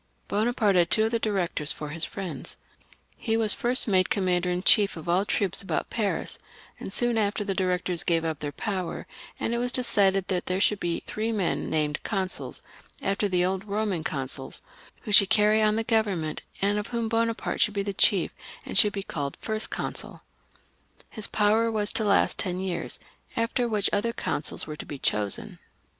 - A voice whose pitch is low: No, high, 200 Hz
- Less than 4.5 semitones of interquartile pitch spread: Yes, average, 3.4 semitones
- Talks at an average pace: Yes, average, 190 wpm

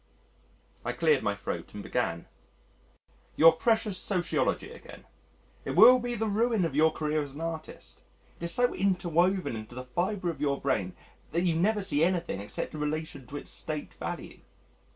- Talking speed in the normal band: Yes, average, 170 wpm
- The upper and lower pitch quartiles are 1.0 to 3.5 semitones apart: No, average, 5.1 semitones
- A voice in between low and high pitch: Yes, medium, 170 Hz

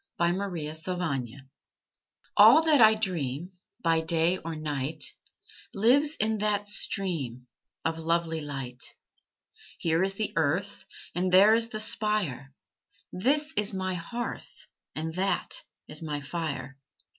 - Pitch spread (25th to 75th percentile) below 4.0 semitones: No, average, 5.2 semitones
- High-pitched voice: No, medium, 175 Hz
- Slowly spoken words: Yes, slow, 130 wpm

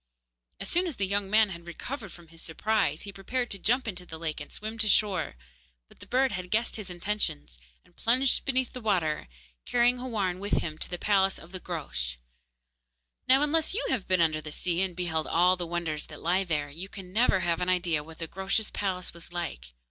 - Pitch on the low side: No, medium, 185 Hz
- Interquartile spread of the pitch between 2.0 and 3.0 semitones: No, average, 4.5 semitones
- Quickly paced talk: Yes, fast, 215 wpm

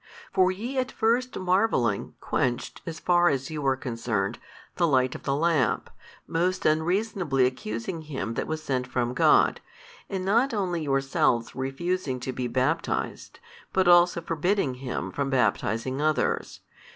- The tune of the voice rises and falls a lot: Yes, wide, 6.1 semitones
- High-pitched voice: No, medium, 150 Hz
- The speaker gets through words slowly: No, average, 145 wpm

